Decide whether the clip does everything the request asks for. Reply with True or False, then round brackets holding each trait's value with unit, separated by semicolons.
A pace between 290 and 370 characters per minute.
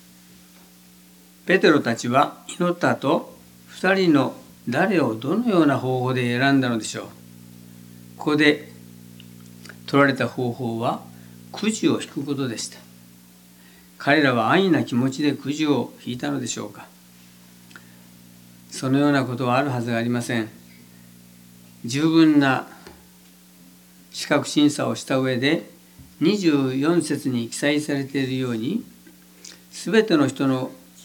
False (230 characters per minute)